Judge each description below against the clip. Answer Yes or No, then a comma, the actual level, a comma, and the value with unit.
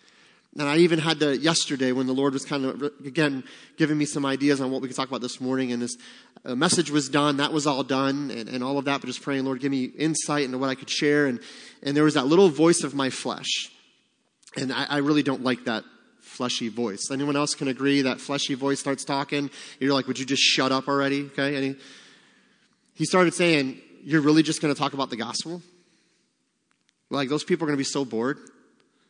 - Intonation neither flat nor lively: No, narrow, 2.2 semitones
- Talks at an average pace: No, fast, 230 wpm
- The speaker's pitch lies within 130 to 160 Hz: Yes, medium, 140 Hz